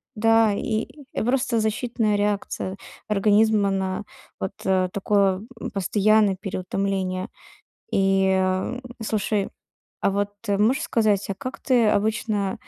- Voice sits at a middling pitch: No, high, 205 Hz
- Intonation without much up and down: Yes, narrow, 2.3 semitones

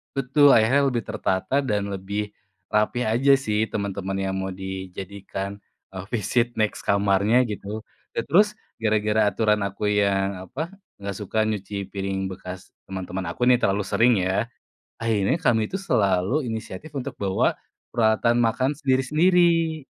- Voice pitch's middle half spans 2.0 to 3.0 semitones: No, average, 4.2 semitones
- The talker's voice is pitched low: Yes, low, 105 Hz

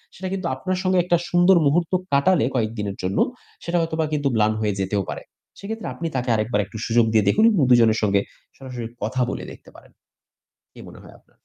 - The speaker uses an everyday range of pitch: No, wide, 8.2 semitones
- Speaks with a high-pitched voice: No, low, 130 Hz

